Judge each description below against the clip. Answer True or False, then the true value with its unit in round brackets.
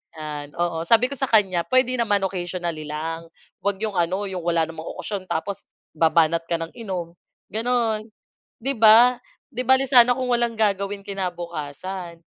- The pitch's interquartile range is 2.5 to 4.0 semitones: False (5.2 semitones)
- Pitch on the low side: False (190 Hz)